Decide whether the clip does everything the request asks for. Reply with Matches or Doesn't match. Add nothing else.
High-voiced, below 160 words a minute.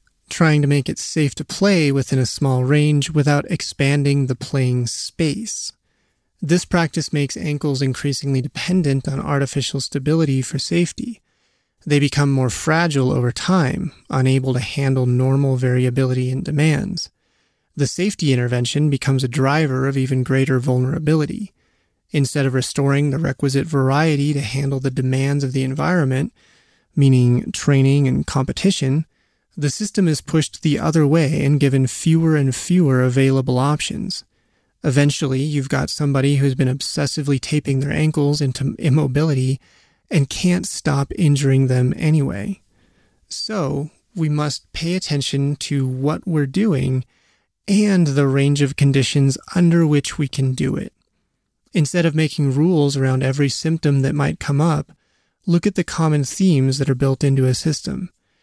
Doesn't match